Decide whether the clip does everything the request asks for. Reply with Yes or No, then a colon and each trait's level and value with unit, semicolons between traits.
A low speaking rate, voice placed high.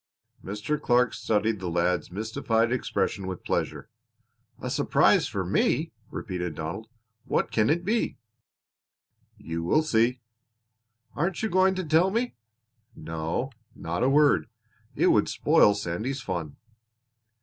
No: slow, 125 wpm; low, 110 Hz